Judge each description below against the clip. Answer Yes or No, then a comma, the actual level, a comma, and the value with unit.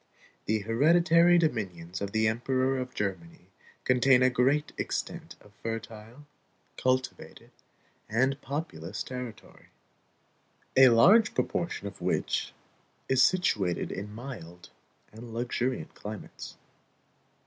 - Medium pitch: No, low, 120 Hz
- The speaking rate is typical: No, slow, 105 wpm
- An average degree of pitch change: Yes, average, 4.2 semitones